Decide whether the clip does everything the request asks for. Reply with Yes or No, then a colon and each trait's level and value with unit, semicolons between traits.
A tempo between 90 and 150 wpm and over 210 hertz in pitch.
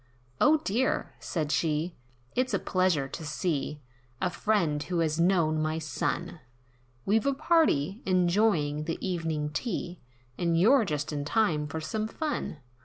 No: average, 140 wpm; medium, 170 Hz